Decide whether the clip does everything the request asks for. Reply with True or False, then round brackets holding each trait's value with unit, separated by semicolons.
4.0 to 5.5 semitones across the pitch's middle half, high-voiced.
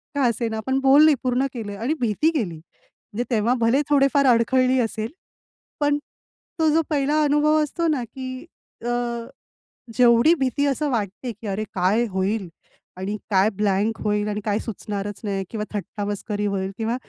True (4.7 semitones; 230 Hz)